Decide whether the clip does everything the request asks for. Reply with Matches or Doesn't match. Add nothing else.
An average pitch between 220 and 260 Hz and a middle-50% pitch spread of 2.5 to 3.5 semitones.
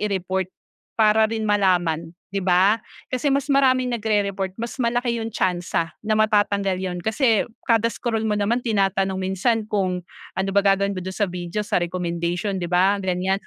Doesn't match